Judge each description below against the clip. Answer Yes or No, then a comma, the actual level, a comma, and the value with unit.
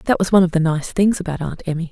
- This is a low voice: No, medium, 175 Hz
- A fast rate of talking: Yes, fast, 315 wpm